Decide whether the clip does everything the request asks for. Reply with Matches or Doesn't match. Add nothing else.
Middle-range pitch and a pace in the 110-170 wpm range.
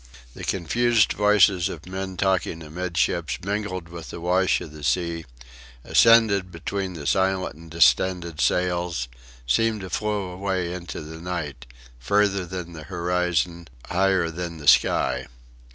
Doesn't match